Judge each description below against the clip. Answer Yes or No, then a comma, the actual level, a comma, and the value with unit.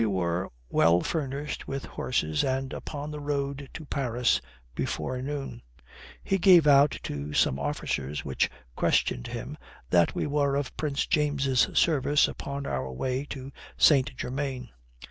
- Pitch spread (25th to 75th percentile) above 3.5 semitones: Yes, wide, 5.4 semitones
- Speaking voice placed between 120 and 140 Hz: Yes, low, 135 Hz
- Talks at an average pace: Yes, average, 145 wpm